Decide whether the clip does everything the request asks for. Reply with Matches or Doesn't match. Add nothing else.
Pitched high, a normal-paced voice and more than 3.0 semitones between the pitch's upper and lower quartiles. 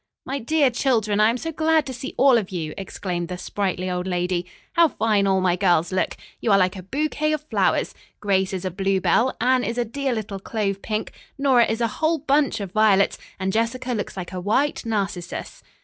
Doesn't match